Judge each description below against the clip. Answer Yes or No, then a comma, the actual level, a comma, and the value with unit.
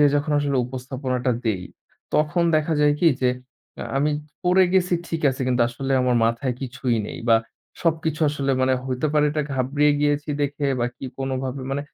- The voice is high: No, medium, 140 Hz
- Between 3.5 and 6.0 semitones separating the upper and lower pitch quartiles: No, average, 2.7 semitones